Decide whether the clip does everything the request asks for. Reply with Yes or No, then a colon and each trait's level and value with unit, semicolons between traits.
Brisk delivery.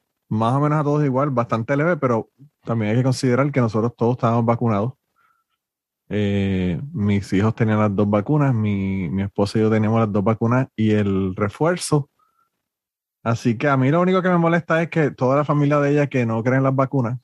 Yes: fast, 200 wpm